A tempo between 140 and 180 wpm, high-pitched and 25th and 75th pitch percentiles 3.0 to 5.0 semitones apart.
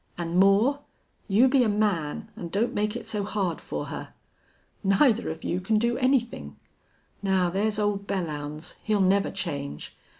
Yes: average, 160 wpm; high, 200 Hz; average, 3.7 semitones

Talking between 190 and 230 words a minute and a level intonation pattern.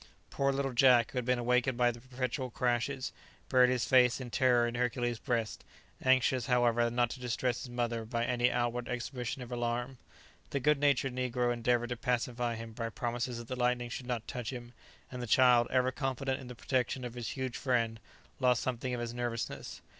Yes: average, 200 wpm; narrow, 1.2 semitones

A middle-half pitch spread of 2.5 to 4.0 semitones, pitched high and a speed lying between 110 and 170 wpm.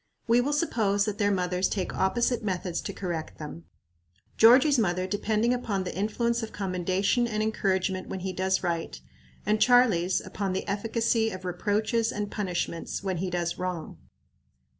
Yes: average, 3.5 semitones; high, 200 Hz; average, 160 wpm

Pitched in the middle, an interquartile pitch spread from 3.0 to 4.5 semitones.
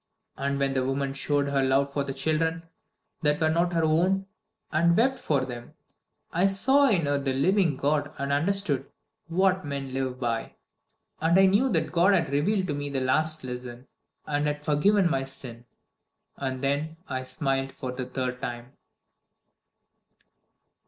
Yes: medium, 145 Hz; average, 4.0 semitones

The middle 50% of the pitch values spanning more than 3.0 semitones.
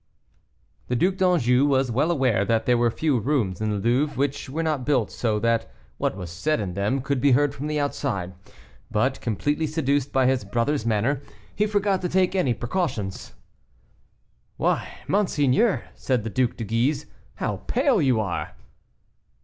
Yes: average, 4.9 semitones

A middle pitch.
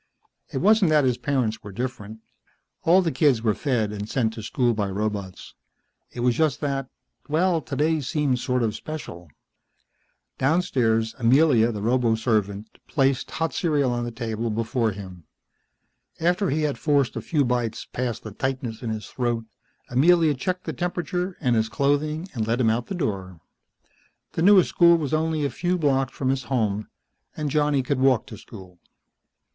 No: low, 130 Hz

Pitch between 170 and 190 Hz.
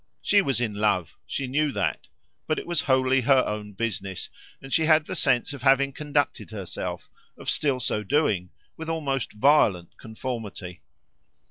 No: low, 130 Hz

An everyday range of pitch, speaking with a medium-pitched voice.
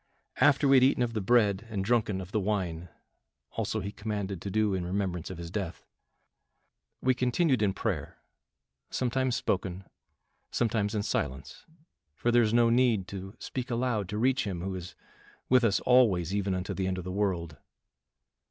No: average, 4.3 semitones; low, 105 Hz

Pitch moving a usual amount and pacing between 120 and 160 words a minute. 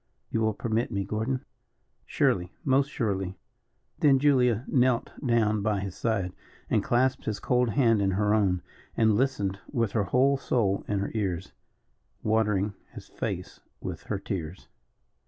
Yes: average, 3.9 semitones; average, 150 wpm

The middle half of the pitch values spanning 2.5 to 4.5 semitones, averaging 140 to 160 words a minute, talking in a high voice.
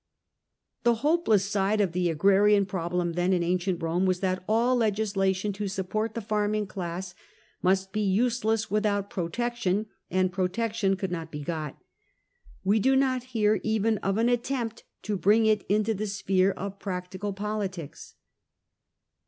Yes: average, 2.8 semitones; average, 150 wpm; high, 200 Hz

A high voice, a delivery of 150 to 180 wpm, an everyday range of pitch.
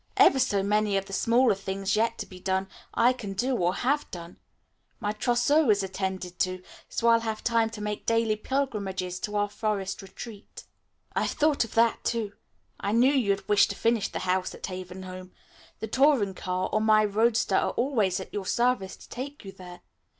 No: high, 210 Hz; average, 195 wpm; average, 3.5 semitones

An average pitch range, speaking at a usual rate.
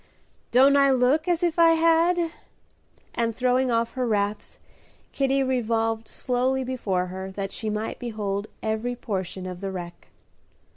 Yes: average, 4.4 semitones; average, 145 wpm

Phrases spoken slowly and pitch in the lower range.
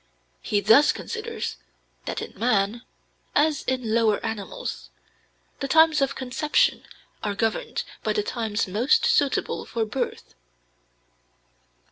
No: slow, 115 wpm; high, 240 Hz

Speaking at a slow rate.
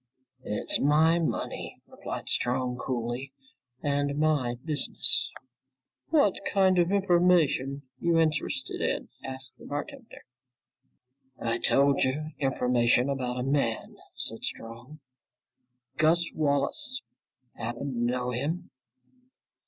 Yes: slow, 105 wpm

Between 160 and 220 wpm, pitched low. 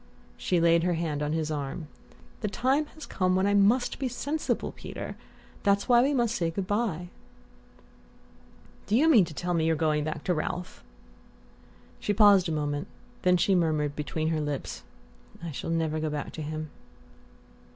No: average, 175 wpm; medium, 170 Hz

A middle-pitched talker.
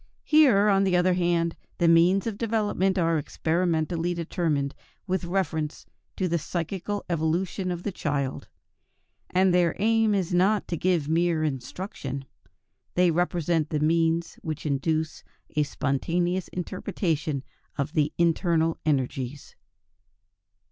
Yes: medium, 170 Hz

